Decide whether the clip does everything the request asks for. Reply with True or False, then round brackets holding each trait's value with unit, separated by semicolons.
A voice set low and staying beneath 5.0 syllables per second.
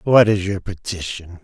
True (95 Hz; 4.5 syllables/s)